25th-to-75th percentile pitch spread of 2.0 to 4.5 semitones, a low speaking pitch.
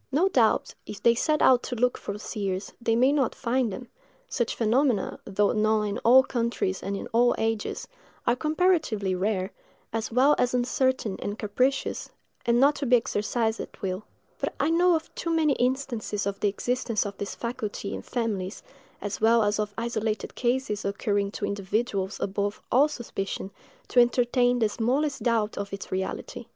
No: average, 3.7 semitones; high, 230 Hz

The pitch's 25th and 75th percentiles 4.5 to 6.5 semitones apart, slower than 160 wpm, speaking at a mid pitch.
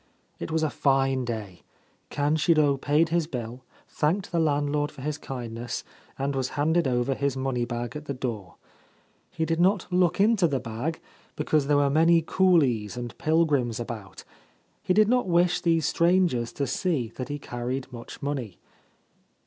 No: average, 4.9 semitones; average, 165 wpm; medium, 145 Hz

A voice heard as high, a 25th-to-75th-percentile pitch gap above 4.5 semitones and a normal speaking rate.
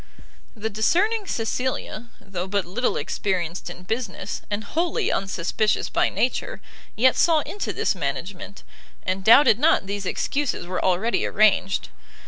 No: high, 205 Hz; average, 5.2 semitones; slow, 130 wpm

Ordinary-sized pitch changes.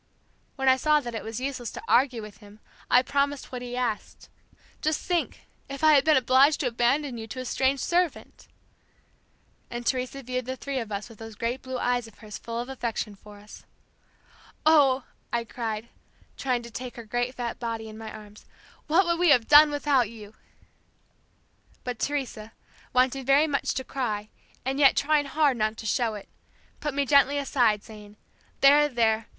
Yes: average, 3.8 semitones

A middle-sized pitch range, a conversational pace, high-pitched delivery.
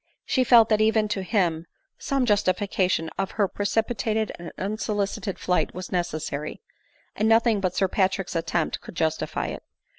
Yes: average, 3.5 semitones; average, 150 wpm; high, 195 Hz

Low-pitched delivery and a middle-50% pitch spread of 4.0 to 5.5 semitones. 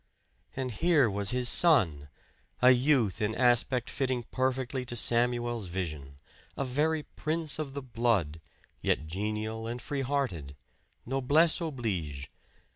Yes: low, 120 Hz; average, 4.7 semitones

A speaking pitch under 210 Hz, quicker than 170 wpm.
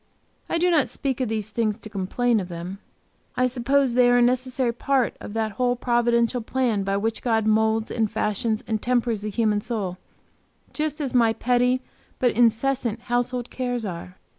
No: high, 235 Hz; average, 180 wpm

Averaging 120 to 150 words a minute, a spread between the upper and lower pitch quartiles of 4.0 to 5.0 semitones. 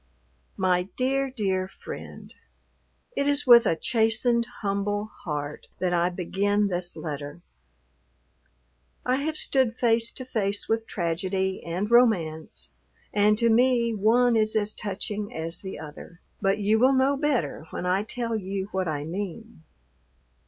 Yes: average, 140 wpm; average, 4.3 semitones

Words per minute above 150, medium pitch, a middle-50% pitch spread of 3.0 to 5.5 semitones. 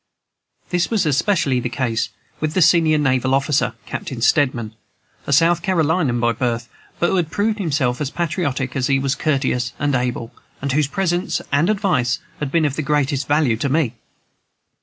Yes: average, 175 wpm; medium, 145 Hz; average, 4.3 semitones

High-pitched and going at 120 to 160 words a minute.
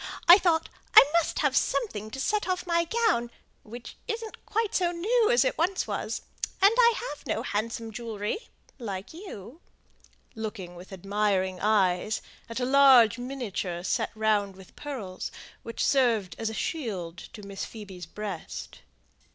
Yes: high, 230 Hz; average, 150 wpm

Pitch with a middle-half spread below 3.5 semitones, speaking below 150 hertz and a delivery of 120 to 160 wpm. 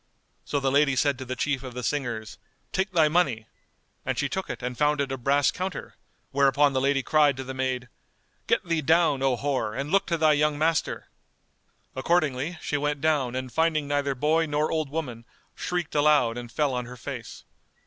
No: average, 2.9 semitones; medium, 140 Hz; average, 200 wpm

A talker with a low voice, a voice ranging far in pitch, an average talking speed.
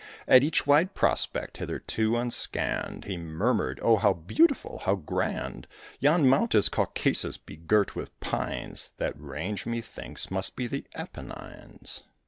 No: low, 110 Hz; wide, 7.1 semitones; slow, 130 wpm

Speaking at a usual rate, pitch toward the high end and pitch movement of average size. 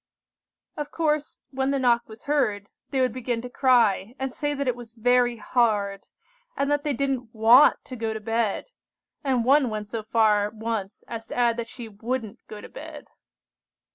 Yes: average, 185 wpm; high, 235 Hz; average, 3.2 semitones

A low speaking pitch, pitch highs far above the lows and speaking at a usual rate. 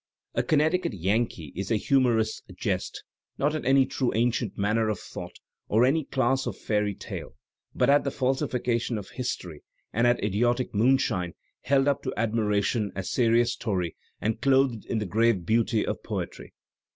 No: low, 115 Hz; average, 3.9 semitones; average, 170 wpm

